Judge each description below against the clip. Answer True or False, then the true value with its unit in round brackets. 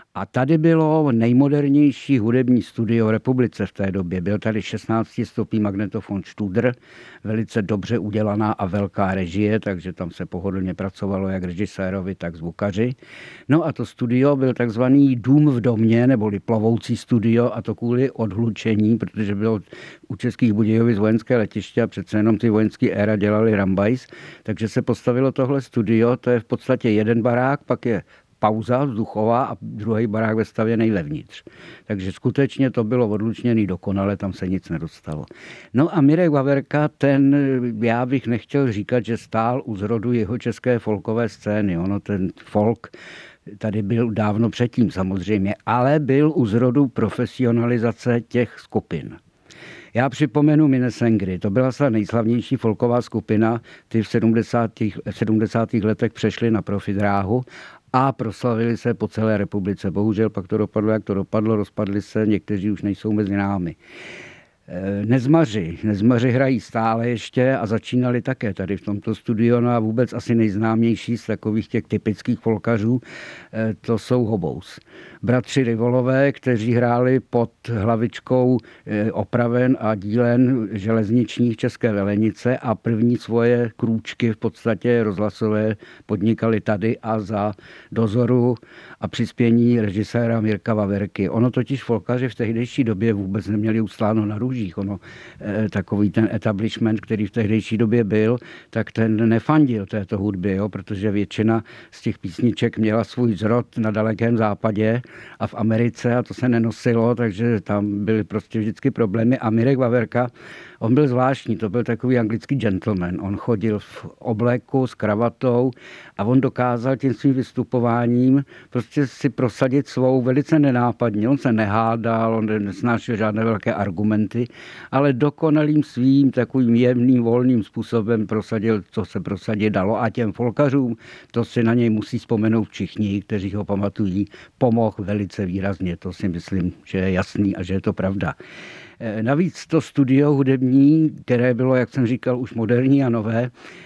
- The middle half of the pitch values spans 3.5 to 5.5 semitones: False (2.6 semitones)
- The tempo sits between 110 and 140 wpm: False (150 wpm)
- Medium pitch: False (115 Hz)